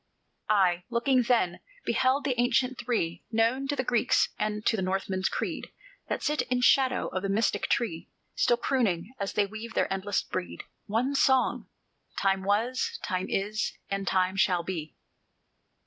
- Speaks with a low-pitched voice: No, high, 215 Hz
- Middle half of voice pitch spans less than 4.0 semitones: No, average, 4.7 semitones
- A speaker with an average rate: Yes, average, 160 wpm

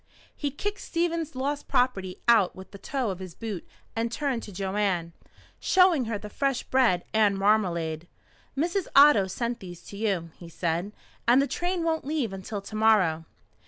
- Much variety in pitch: Yes, wide, 6.6 semitones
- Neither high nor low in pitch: No, high, 220 Hz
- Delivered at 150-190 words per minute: Yes, average, 170 wpm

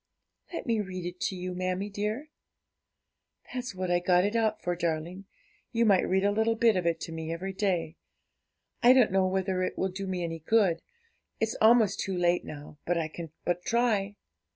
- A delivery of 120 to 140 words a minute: No, average, 195 wpm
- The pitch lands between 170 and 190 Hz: Yes, medium, 185 Hz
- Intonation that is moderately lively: Yes, average, 3.3 semitones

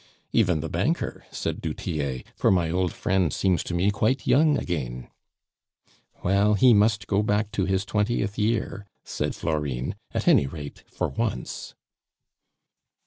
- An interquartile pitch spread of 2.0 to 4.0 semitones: No, average, 4.6 semitones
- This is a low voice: Yes, very low, 95 Hz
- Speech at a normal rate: Yes, average, 145 wpm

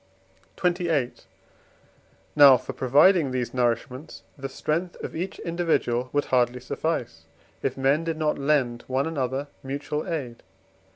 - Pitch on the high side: No, low, 135 Hz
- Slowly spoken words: Yes, slow, 125 wpm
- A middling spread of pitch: Yes, average, 4.1 semitones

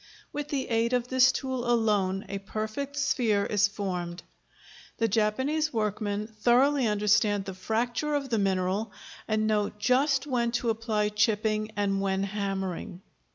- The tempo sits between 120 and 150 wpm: Yes, average, 145 wpm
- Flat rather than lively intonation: No, average, 3.4 semitones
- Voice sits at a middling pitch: No, high, 215 Hz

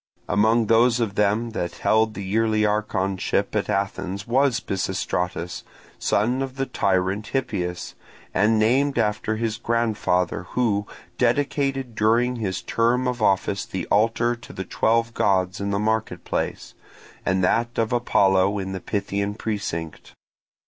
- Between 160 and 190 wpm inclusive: No, average, 140 wpm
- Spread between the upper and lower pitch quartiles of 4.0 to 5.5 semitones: No, average, 3.2 semitones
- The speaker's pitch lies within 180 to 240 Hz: No, low, 110 Hz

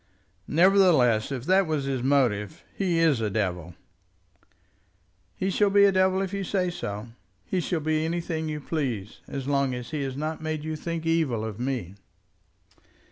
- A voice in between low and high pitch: Yes, medium, 155 Hz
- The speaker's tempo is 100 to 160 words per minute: No, average, 170 wpm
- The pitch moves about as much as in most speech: No, wide, 5.8 semitones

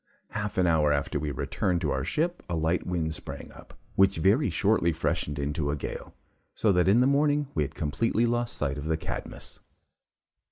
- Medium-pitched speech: No, very low, 85 Hz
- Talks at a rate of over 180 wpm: Yes, average, 195 wpm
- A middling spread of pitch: No, wide, 6.6 semitones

